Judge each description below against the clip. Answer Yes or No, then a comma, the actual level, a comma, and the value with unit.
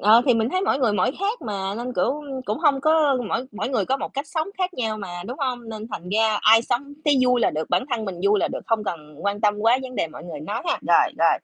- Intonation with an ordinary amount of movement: Yes, average, 4.7 semitones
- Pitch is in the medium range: No, high, 225 Hz